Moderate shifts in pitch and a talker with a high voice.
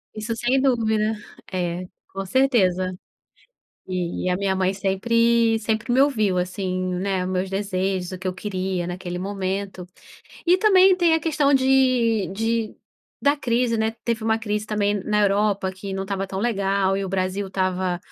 Yes: average, 3.6 semitones; high, 200 Hz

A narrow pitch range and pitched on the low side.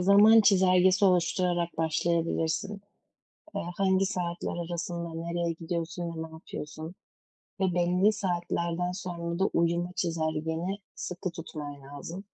No: narrow, 1.9 semitones; medium, 175 Hz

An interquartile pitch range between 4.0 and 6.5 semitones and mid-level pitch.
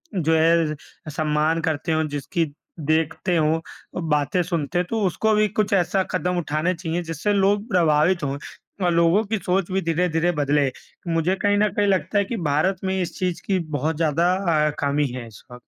No: average, 3.6 semitones; medium, 165 Hz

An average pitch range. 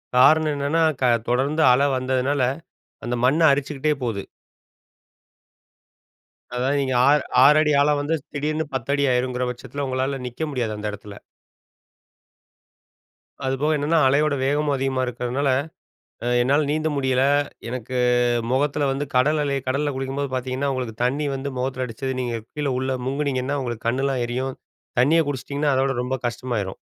No: narrow, 2.3 semitones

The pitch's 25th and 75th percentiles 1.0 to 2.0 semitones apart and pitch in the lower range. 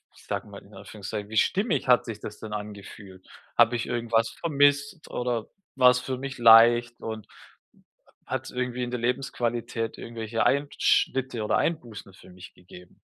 No: average, 2.7 semitones; low, 120 Hz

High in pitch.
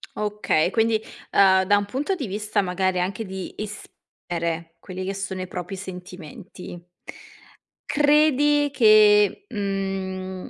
Yes: high, 195 Hz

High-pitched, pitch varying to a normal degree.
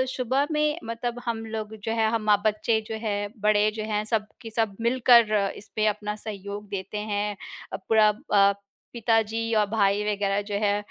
No: high, 215 Hz; narrow, 1.6 semitones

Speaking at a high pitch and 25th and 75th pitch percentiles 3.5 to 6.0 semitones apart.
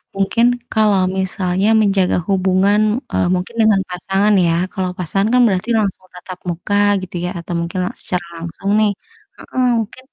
No: high, 195 Hz; narrow, 2.4 semitones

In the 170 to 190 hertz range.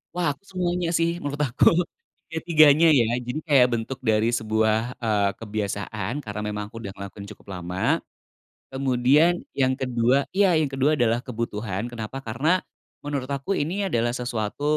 No: low, 125 Hz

